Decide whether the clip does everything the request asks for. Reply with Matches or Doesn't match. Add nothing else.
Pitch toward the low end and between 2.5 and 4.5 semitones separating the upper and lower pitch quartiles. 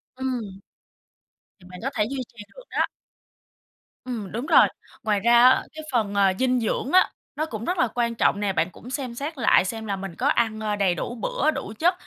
Doesn't match